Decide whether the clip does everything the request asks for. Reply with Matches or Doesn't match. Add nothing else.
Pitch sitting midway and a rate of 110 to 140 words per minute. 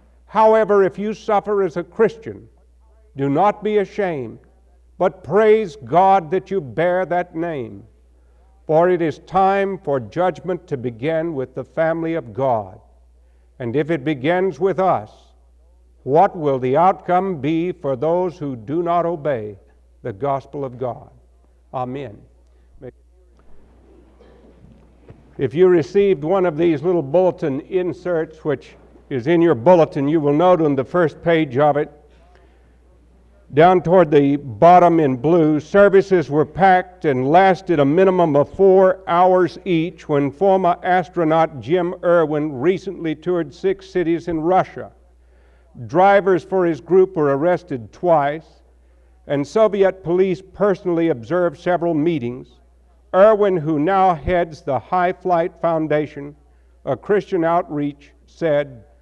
Matches